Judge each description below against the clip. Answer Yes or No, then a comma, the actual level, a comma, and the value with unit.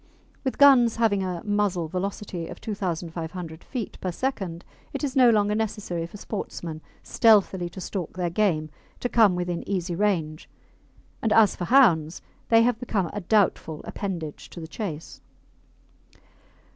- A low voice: No, high, 190 Hz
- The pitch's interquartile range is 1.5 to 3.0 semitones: No, average, 4.3 semitones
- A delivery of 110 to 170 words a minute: Yes, average, 145 wpm